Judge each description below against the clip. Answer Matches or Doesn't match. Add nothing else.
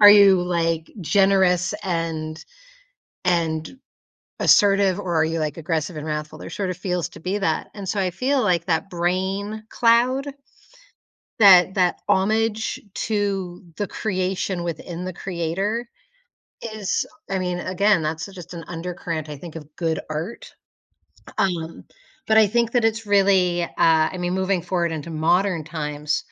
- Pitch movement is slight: Doesn't match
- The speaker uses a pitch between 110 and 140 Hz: Doesn't match